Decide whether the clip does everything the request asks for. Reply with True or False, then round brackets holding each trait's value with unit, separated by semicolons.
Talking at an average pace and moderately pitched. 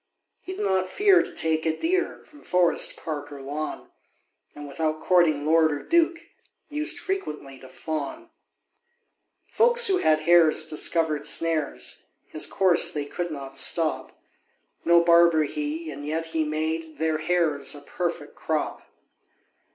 True (145 wpm; 160 Hz)